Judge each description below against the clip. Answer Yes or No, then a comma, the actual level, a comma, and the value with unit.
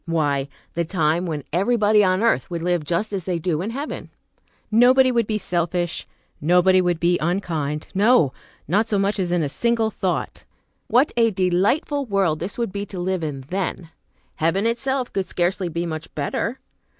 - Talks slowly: No, average, 175 wpm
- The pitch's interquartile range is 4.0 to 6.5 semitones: Yes, average, 4.4 semitones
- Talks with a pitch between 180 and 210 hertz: Yes, medium, 185 Hz